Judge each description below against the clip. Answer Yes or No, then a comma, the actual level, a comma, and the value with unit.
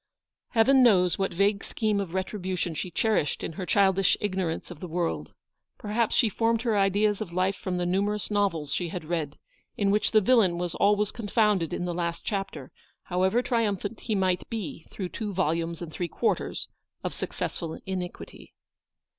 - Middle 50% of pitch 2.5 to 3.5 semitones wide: Yes, average, 3.1 semitones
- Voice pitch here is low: No, high, 190 Hz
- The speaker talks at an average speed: Yes, average, 180 wpm